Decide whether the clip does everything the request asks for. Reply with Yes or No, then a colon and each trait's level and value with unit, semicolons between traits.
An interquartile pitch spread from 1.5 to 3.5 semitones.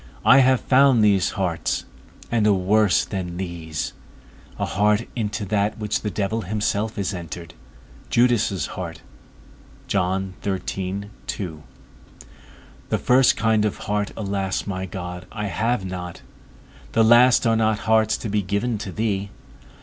Yes: average, 2.9 semitones